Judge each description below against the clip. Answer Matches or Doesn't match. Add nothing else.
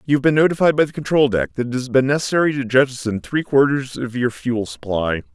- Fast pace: Matches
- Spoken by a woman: Doesn't match